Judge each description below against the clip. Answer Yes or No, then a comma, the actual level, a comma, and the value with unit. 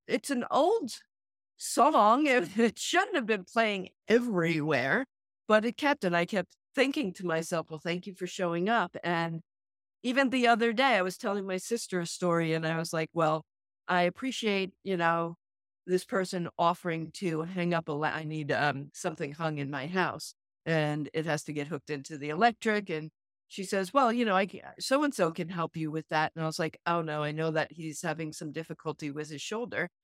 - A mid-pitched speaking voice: Yes, medium, 175 Hz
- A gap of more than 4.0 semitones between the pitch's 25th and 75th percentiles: Yes, average, 4.8 semitones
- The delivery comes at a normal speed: No, fast, 210 wpm